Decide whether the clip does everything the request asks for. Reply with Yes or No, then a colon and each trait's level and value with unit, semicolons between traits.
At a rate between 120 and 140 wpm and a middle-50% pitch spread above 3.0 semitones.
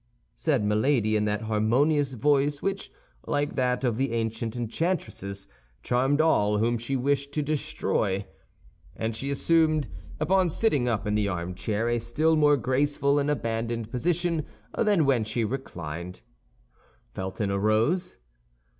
Yes: slow, 135 wpm; average, 5.2 semitones